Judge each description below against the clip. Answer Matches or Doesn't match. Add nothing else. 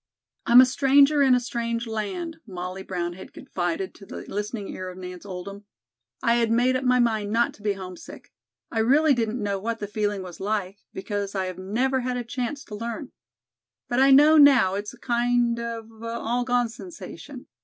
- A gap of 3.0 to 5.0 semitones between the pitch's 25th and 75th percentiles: Matches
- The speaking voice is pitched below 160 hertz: Doesn't match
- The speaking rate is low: Doesn't match